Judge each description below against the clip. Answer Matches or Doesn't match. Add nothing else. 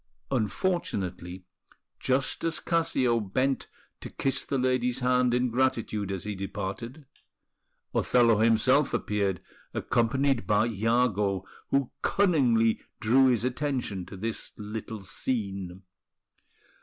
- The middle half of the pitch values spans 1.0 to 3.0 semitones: Doesn't match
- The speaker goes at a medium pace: Doesn't match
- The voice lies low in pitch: Matches